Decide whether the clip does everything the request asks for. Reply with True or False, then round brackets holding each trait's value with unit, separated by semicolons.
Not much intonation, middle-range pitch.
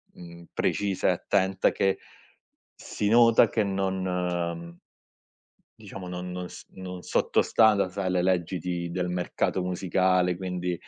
False (1.2 semitones; 90 Hz)